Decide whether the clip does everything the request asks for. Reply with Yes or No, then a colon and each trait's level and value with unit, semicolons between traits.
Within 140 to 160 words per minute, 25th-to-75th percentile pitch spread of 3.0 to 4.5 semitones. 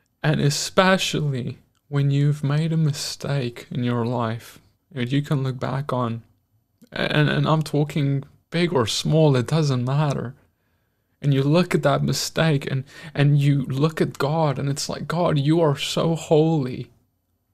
Yes: average, 155 wpm; average, 3.8 semitones